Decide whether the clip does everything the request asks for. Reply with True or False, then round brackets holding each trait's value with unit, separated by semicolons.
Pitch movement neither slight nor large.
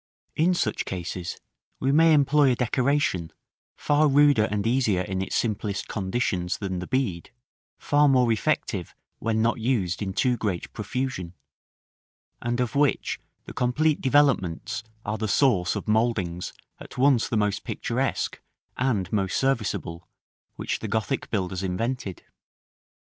False (5.7 semitones)